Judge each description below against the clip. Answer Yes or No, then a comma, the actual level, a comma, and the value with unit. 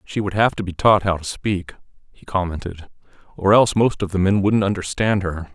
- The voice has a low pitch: Yes, very low, 95 Hz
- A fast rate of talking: Yes, fast, 215 wpm